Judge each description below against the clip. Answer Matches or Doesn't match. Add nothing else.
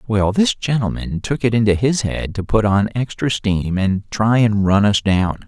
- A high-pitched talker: Doesn't match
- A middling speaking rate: Doesn't match